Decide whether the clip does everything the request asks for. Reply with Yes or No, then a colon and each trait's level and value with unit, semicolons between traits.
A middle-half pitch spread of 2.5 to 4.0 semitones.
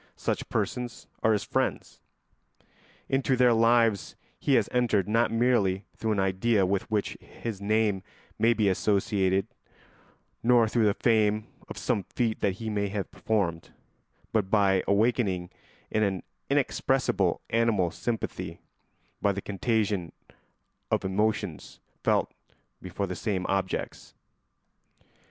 Yes: average, 2.9 semitones